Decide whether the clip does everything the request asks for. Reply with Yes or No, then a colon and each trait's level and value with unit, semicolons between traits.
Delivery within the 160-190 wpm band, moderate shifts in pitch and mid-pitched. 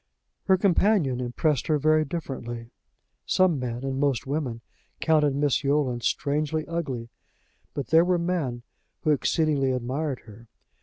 No: slow, 135 wpm; average, 3.9 semitones; medium, 145 Hz